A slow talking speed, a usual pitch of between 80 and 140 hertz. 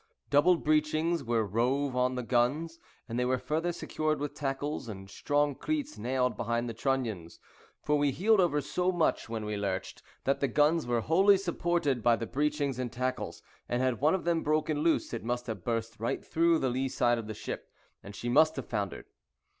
No: average, 200 wpm; low, 135 Hz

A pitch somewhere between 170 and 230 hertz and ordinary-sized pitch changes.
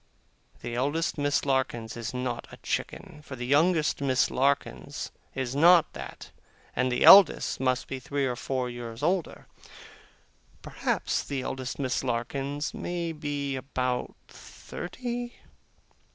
No: low, 135 Hz; average, 3.0 semitones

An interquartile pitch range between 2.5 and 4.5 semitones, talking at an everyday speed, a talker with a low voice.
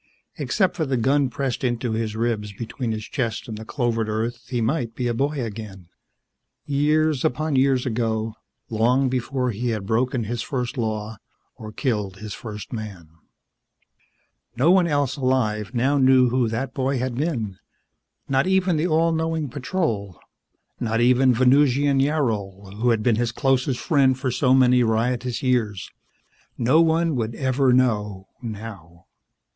Yes: average, 3.6 semitones; average, 155 wpm; low, 125 Hz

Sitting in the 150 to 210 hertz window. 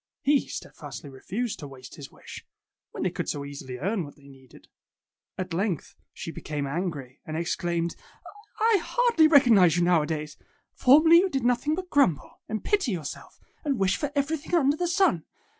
Yes: high, 190 Hz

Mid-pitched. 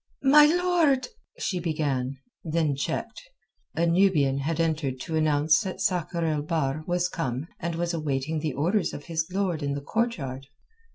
Yes: medium, 160 Hz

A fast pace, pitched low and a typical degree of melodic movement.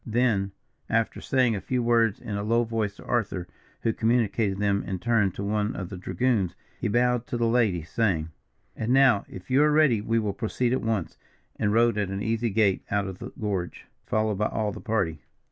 Yes: fast, 210 wpm; low, 110 Hz; average, 3.0 semitones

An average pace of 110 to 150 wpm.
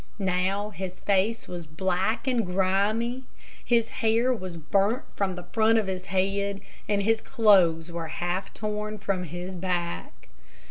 Yes: average, 145 wpm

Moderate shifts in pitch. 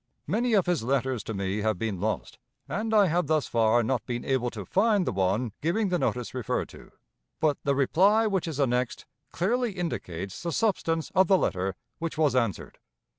No: wide, 8.4 semitones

